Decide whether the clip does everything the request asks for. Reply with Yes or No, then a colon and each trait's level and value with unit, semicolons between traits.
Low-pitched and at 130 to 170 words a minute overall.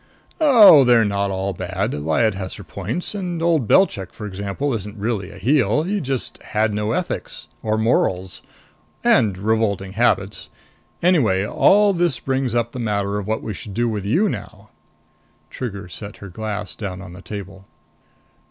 Yes: low, 105 Hz; average, 165 wpm